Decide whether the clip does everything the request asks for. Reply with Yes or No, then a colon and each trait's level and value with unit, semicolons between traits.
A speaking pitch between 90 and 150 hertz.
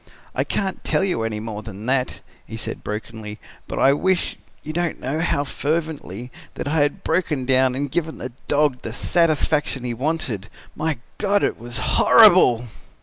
Yes: low, 135 Hz